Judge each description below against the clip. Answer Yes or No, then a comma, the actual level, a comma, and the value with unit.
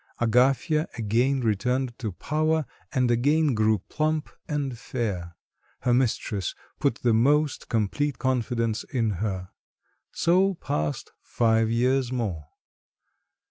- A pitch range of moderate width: Yes, average, 4.2 semitones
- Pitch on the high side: No, low, 120 Hz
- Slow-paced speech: Yes, slow, 110 wpm